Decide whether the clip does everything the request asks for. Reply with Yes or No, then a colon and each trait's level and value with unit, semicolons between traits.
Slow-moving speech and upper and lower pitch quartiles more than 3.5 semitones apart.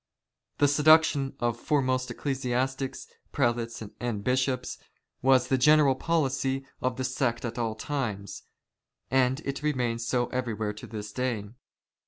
No: slow, 130 wpm; narrow, 2.4 semitones